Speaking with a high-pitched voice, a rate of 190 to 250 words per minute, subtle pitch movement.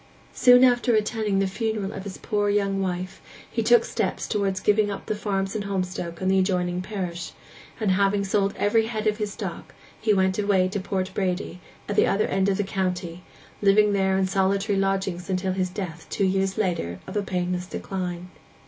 Yes: high, 195 Hz; average, 195 wpm; narrow, 1.9 semitones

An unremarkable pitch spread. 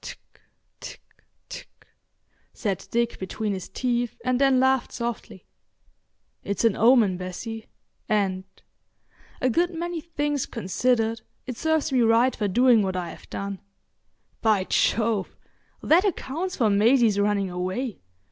Yes: average, 4.6 semitones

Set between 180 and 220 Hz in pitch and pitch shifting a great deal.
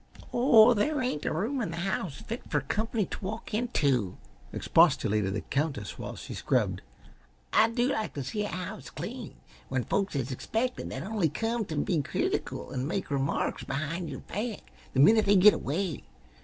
Yes: medium, 185 Hz; wide, 7.7 semitones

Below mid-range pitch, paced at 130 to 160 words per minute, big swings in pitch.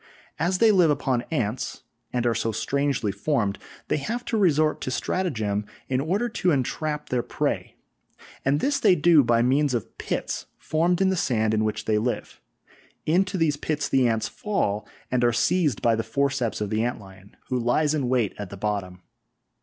No: low, 130 Hz; average, 185 wpm; wide, 6.0 semitones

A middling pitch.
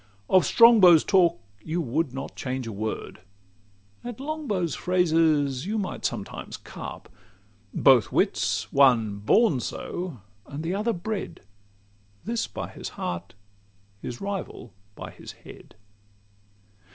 Yes: medium, 165 Hz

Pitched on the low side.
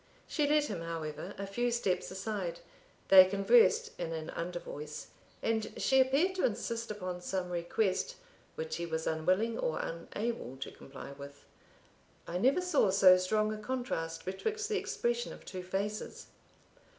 No: high, 195 Hz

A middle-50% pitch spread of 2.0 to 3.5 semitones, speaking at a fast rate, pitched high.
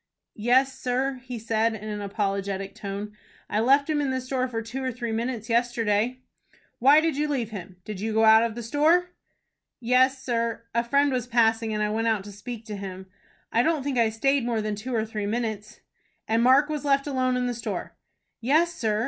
Yes: average, 3.2 semitones; fast, 210 wpm; high, 235 Hz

